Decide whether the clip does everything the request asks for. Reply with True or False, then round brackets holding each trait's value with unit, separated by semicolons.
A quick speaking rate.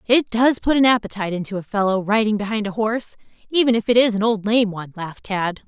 True (230 wpm)